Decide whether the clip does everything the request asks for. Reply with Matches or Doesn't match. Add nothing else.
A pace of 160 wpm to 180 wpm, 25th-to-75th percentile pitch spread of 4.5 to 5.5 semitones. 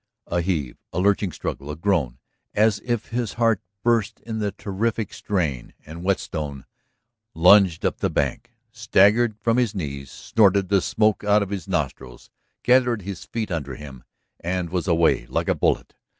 Matches